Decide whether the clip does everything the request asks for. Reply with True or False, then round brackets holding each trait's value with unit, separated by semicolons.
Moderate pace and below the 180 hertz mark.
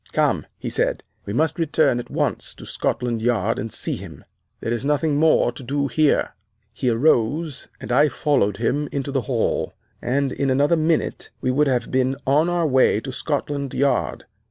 True (180 wpm; 135 Hz)